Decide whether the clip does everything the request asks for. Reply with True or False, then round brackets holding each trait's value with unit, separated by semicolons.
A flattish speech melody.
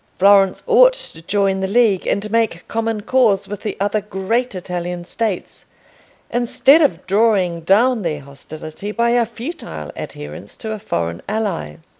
False (4.6 semitones)